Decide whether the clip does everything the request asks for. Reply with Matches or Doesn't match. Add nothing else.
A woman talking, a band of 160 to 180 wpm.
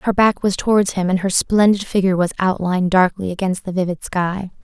Doesn't match